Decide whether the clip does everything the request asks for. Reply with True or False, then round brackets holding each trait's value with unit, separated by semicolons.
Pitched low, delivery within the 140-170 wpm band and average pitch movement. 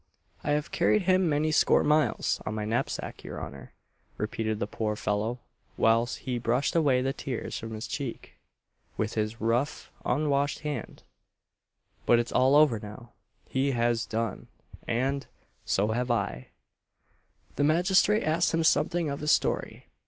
True (125 Hz; 150 wpm; 4.9 semitones)